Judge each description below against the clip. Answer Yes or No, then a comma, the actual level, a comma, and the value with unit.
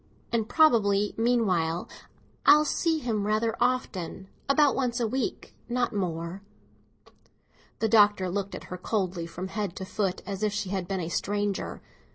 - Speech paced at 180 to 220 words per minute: No, average, 160 wpm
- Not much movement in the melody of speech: No, average, 3.8 semitones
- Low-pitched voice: No, high, 205 Hz